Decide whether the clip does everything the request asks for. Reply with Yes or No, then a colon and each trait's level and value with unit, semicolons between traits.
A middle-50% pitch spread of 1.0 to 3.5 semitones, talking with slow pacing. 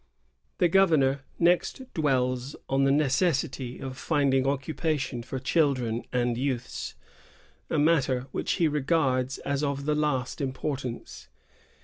Yes: average, 2.7 semitones; slow, 130 wpm